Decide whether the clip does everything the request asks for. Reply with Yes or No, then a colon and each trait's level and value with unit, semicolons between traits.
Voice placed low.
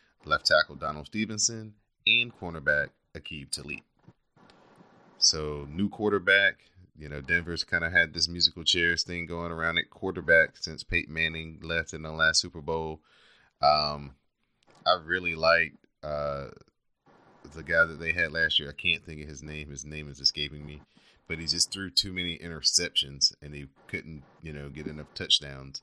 Yes: very low, 80 Hz